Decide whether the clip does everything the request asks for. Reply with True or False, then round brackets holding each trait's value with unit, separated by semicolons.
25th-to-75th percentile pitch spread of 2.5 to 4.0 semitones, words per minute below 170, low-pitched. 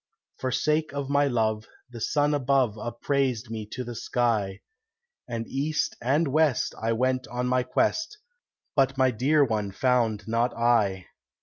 True (3.4 semitones; 150 wpm; 125 Hz)